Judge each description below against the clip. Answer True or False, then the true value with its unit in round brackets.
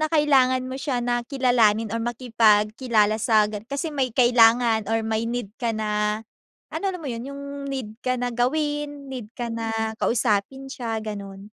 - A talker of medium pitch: False (235 Hz)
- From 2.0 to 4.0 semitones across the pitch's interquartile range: True (3.1 semitones)